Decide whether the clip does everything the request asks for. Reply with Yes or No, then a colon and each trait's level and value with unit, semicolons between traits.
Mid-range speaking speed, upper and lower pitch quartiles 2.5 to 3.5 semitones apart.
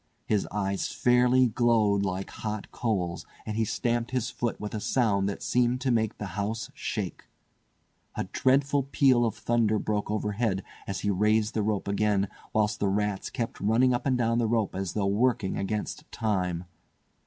Yes: average, 175 wpm; average, 2.9 semitones